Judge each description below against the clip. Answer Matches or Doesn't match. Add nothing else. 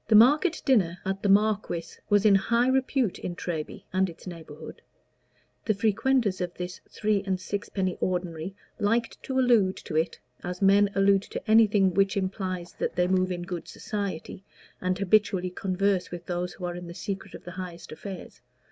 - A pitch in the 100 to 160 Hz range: Doesn't match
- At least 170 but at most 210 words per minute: Matches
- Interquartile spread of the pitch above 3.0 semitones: Doesn't match